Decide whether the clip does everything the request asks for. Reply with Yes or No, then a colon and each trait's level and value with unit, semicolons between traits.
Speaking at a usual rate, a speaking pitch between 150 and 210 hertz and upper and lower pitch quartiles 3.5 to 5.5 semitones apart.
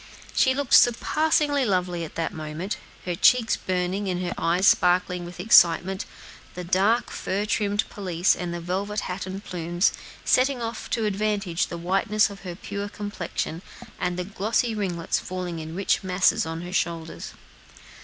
No: average, 160 wpm; medium, 185 Hz; average, 3.0 semitones